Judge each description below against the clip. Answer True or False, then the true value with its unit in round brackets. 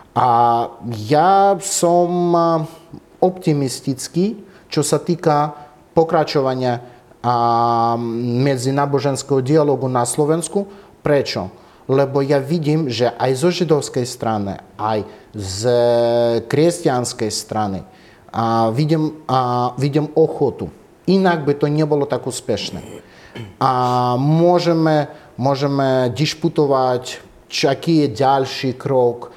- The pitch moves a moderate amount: True (4.4 semitones)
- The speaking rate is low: True (90 wpm)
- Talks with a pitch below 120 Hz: False (140 Hz)